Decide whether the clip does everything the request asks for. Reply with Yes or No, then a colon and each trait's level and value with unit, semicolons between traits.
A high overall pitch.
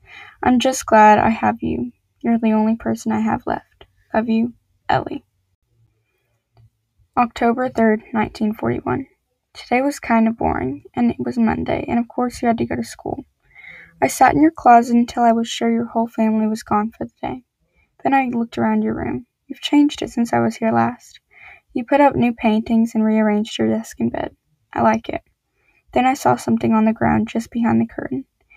Yes: high, 220 Hz